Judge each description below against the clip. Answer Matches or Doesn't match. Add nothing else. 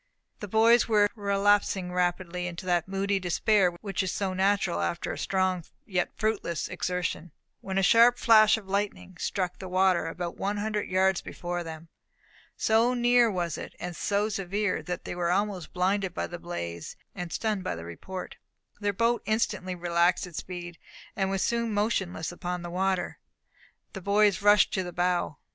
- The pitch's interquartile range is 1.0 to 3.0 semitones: Matches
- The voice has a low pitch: Doesn't match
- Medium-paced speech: Matches